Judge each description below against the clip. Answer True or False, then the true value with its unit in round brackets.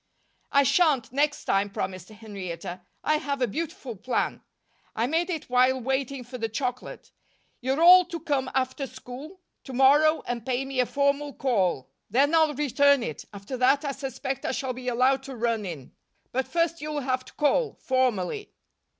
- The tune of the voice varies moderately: True (3.3 semitones)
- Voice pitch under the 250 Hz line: False (265 Hz)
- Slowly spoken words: False (175 wpm)